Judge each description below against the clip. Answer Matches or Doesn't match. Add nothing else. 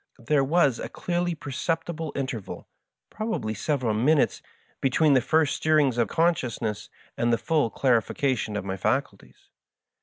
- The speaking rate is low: Doesn't match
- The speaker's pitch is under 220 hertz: Matches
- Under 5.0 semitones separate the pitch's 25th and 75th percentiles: Doesn't match